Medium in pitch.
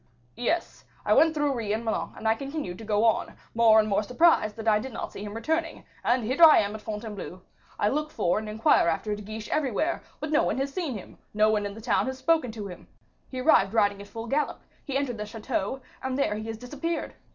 No: high, 225 Hz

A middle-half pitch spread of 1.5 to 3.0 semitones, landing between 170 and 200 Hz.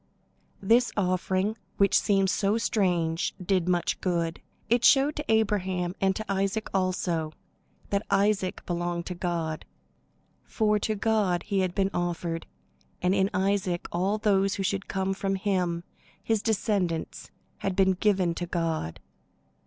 Yes: narrow, 2.5 semitones; high, 190 Hz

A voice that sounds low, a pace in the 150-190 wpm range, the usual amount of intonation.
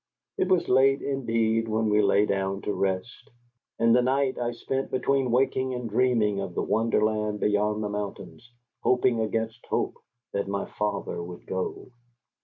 Yes: low, 110 Hz; average, 160 wpm; average, 3.3 semitones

